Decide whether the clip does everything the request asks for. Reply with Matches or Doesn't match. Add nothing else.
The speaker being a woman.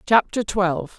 Matches